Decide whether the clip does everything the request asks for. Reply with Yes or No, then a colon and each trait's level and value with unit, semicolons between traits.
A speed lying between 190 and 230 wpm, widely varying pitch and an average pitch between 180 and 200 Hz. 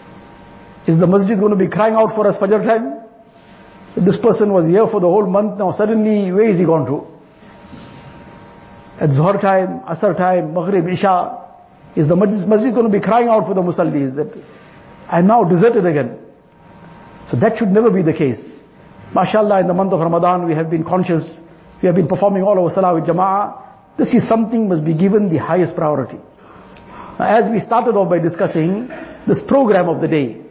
No: average, 195 wpm; average, 4.0 semitones; high, 190 Hz